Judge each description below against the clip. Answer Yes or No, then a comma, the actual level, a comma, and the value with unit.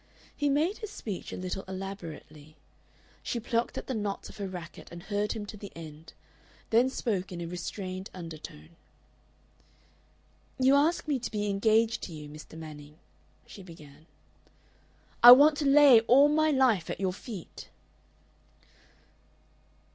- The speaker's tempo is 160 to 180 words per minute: No, average, 145 wpm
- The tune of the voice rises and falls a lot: Yes, wide, 6.7 semitones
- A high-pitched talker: Yes, high, 200 Hz